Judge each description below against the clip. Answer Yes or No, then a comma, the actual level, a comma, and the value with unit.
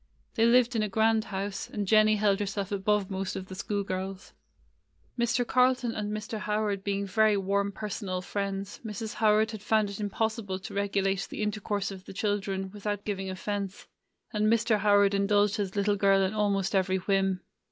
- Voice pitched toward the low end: No, high, 205 Hz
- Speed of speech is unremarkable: Yes, average, 185 wpm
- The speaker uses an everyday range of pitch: No, narrow, 1.6 semitones